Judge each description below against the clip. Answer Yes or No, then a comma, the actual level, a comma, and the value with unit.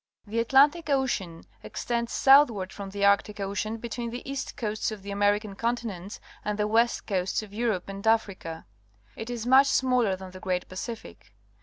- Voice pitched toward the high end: Yes, high, 215 Hz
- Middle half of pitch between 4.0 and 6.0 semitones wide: No, average, 3.3 semitones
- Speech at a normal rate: Yes, average, 170 wpm